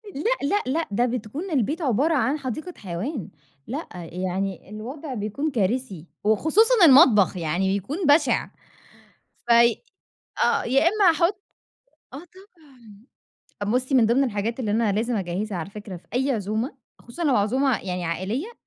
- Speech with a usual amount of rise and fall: No, wide, 6.1 semitones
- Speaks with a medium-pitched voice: No, high, 240 Hz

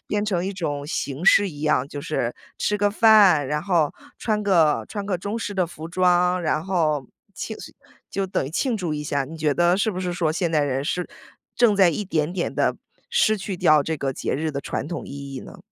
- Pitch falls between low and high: Yes, medium, 175 Hz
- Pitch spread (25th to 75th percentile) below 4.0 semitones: No, average, 4.7 semitones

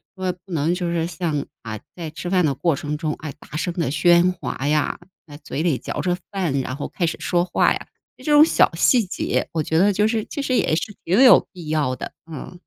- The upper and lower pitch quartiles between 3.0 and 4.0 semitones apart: Yes, average, 3.3 semitones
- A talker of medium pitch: Yes, medium, 170 Hz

